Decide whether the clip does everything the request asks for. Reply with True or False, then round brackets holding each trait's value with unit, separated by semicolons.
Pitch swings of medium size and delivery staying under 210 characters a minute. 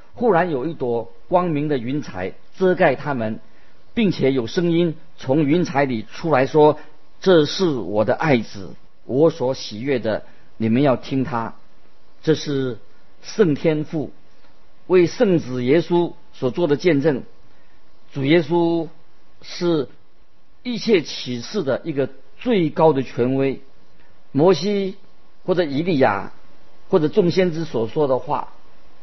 True (4.6 semitones; 185 characters per minute)